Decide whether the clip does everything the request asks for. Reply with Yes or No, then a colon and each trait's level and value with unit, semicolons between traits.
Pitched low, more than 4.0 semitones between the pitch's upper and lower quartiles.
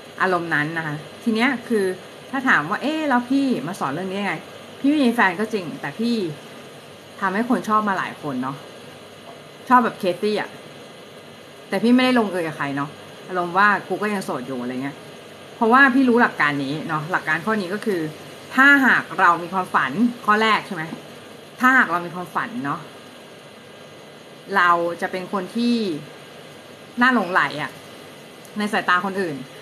No: high, 200 Hz; wide, 5.5 semitones